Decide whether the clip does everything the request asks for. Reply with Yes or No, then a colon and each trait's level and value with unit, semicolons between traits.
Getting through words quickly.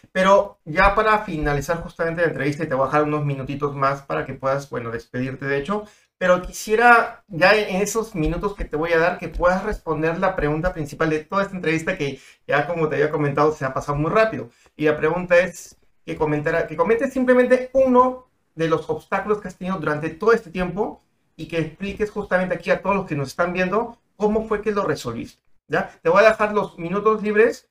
Yes: fast, 210 wpm